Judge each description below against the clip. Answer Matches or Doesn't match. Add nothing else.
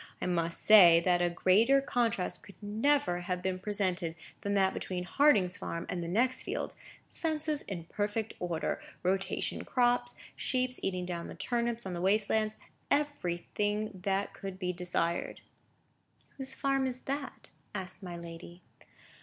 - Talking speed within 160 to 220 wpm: Doesn't match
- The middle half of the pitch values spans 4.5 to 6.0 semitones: Matches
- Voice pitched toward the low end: Doesn't match